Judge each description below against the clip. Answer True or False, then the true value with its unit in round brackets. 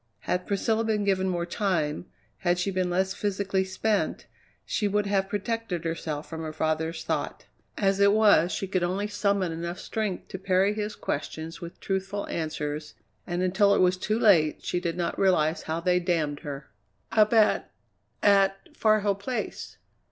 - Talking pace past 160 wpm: True (170 wpm)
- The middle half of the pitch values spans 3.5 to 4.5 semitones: False (3.1 semitones)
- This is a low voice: False (190 Hz)